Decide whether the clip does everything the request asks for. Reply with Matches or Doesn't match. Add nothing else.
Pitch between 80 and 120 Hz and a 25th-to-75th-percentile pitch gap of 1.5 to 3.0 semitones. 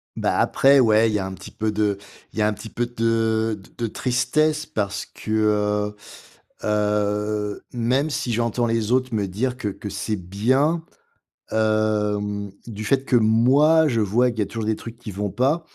Matches